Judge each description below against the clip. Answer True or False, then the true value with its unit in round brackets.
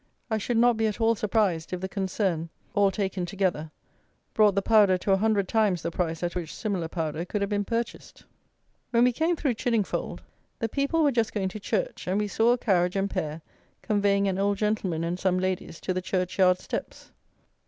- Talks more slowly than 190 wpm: False (205 wpm)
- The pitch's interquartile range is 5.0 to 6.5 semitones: False (3.2 semitones)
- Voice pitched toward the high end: True (200 Hz)